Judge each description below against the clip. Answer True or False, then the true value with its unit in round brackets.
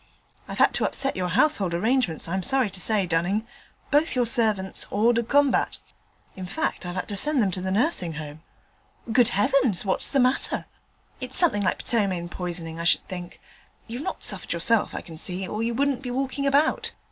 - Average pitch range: False (6.2 semitones)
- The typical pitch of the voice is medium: False (210 Hz)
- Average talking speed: True (195 wpm)